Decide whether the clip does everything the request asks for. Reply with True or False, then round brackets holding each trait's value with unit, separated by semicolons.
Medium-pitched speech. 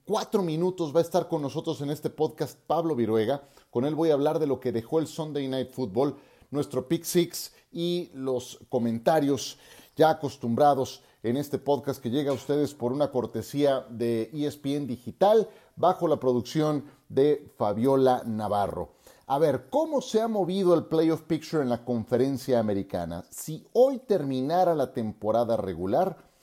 True (145 Hz)